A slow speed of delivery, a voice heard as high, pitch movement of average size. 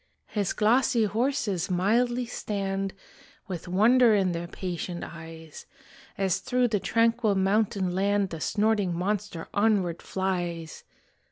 Yes: slow, 115 wpm; high, 195 Hz; average, 3.6 semitones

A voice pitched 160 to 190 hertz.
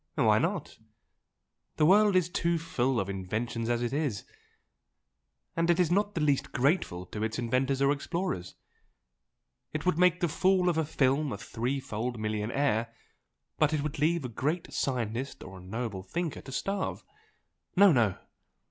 No: medium, 140 Hz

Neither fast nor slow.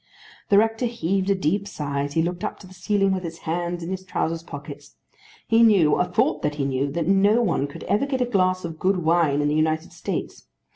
No: fast, 235 wpm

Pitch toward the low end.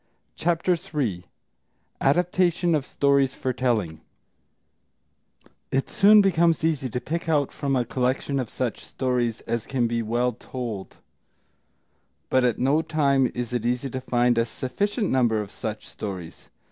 Yes: low, 130 Hz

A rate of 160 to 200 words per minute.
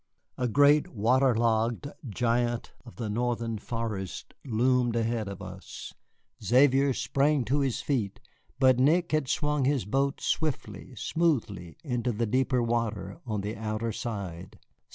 No: slow, 135 wpm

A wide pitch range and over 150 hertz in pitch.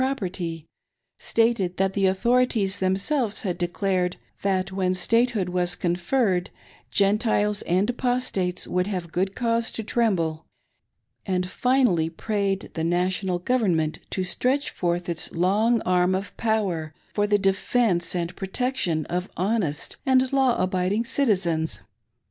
No: average, 4.3 semitones; high, 190 Hz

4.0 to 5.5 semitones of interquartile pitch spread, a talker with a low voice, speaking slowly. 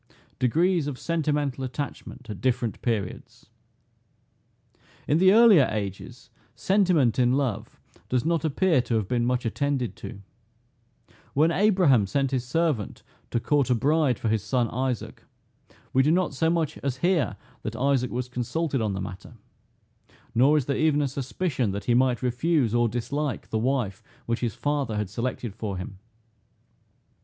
No: average, 4.3 semitones; low, 130 Hz; average, 155 wpm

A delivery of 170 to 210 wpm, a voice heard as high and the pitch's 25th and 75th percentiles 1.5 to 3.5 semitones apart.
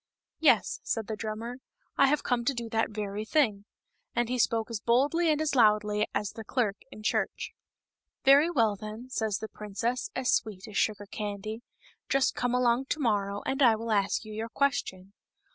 Yes: average, 195 wpm; high, 225 Hz; average, 3.1 semitones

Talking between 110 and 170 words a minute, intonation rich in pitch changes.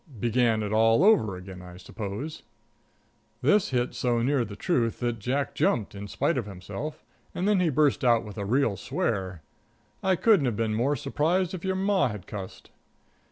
No: average, 180 wpm; wide, 6.7 semitones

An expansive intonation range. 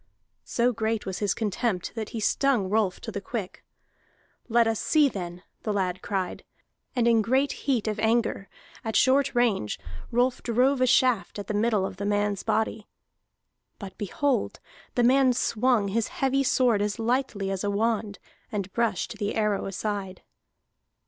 No: average, 3.3 semitones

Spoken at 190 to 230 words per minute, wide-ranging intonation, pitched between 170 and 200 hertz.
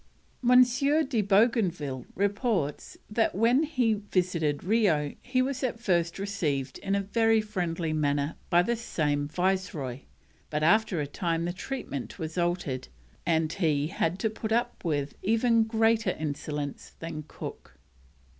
No: average, 140 wpm; wide, 6.5 semitones; medium, 185 Hz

